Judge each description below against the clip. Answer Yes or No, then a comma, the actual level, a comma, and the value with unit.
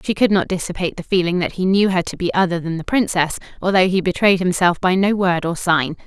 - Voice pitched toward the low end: No, medium, 180 Hz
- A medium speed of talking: No, fast, 245 wpm